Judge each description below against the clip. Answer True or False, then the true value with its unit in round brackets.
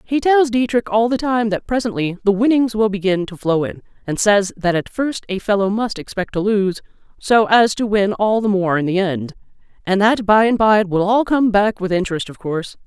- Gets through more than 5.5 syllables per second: False (5.3 syllables/s)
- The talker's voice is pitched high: True (205 Hz)